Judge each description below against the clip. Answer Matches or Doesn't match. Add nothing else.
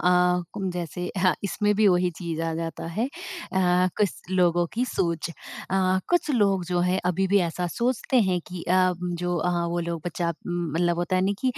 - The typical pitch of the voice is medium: Matches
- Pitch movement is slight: Matches